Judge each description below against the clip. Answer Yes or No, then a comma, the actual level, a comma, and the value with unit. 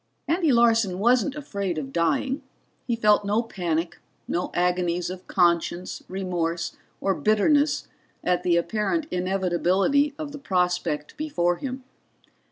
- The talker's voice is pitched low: No, high, 190 Hz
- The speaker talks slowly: Yes, slow, 125 wpm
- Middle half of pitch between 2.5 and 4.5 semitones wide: No, wide, 5.6 semitones